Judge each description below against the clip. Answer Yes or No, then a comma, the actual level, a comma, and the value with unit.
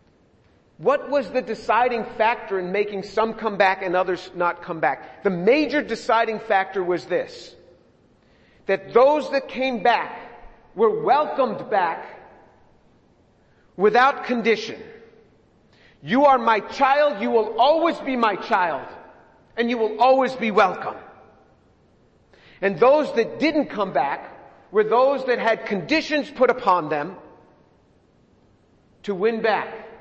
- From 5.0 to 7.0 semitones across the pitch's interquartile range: No, average, 4.6 semitones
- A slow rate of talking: Yes, slow, 130 wpm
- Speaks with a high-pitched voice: Yes, high, 225 Hz